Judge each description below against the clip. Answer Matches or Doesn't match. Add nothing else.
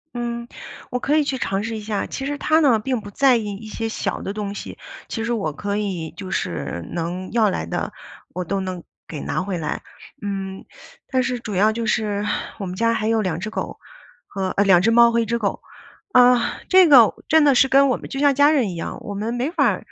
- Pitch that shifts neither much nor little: Matches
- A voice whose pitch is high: Matches